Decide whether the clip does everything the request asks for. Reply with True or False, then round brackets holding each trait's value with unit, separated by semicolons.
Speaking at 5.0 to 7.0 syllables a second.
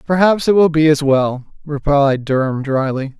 False (4.6 syllables/s)